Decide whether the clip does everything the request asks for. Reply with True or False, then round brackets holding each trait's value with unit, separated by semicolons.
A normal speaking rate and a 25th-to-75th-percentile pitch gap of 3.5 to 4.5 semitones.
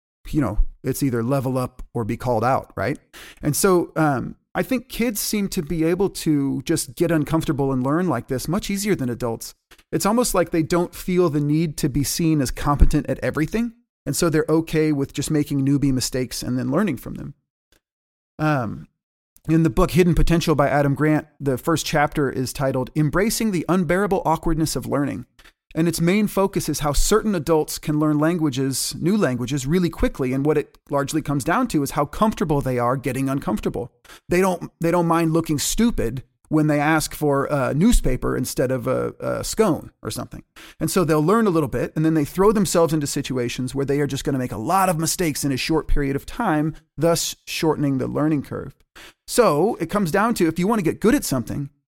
False (210 wpm; 4.0 semitones)